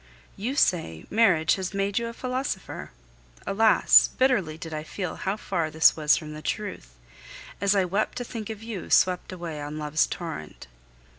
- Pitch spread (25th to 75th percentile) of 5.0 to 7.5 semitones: Yes, wide, 5.4 semitones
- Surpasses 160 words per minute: Yes, average, 170 wpm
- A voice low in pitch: No, medium, 185 Hz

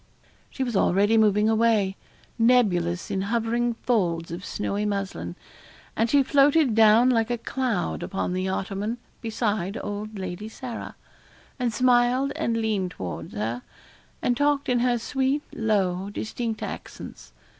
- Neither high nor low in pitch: No, high, 220 Hz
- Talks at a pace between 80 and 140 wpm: Yes, slow, 135 wpm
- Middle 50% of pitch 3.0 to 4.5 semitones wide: Yes, average, 3.9 semitones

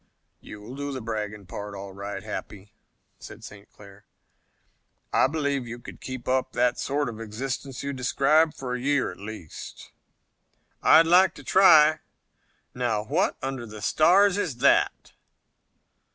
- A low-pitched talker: Yes, low, 125 Hz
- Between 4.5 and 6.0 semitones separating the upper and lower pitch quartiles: Yes, average, 5.1 semitones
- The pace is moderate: Yes, average, 145 wpm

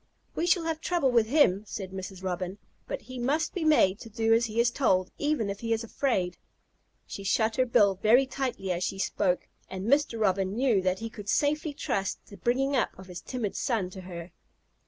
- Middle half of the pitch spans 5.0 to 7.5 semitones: Yes, wide, 5.6 semitones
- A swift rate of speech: Yes, fast, 210 wpm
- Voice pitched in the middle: No, high, 225 Hz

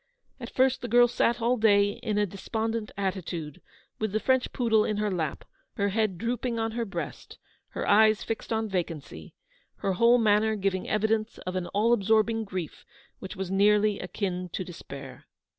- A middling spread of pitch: Yes, average, 3.0 semitones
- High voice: Yes, high, 210 Hz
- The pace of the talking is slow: No, average, 175 wpm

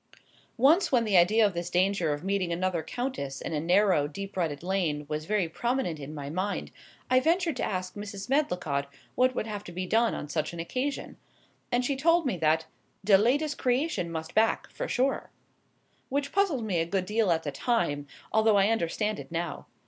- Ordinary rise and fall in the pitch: No, wide, 6.8 semitones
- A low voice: No, high, 195 Hz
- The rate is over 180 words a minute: Yes, average, 195 wpm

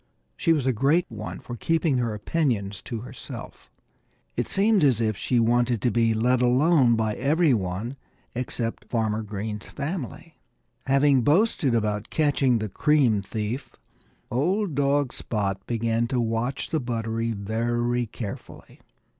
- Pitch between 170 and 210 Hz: No, low, 120 Hz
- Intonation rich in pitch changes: No, average, 4.1 semitones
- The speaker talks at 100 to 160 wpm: Yes, average, 140 wpm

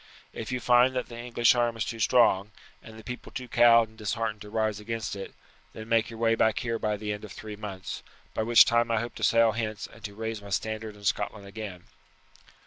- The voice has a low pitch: Yes, low, 110 Hz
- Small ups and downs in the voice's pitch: Yes, narrow, 1.7 semitones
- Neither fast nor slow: No, fast, 230 wpm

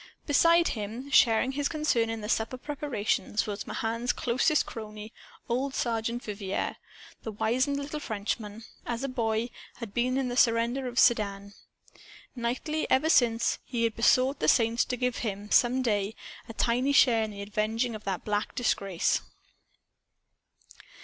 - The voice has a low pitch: No, high, 235 Hz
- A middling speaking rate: Yes, average, 150 wpm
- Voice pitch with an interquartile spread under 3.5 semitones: Yes, average, 3.0 semitones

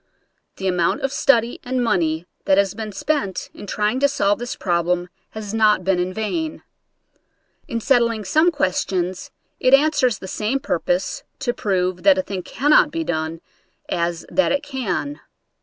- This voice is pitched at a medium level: No, high, 215 Hz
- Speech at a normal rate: Yes, average, 160 wpm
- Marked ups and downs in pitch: Yes, wide, 7.0 semitones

